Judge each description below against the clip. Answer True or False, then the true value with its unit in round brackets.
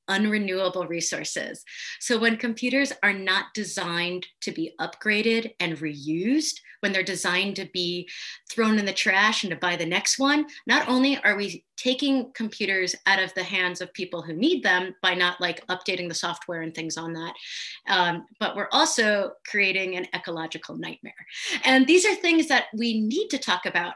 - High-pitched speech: True (195 Hz)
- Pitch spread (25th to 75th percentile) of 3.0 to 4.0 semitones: False (4.6 semitones)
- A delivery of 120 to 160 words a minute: False (180 wpm)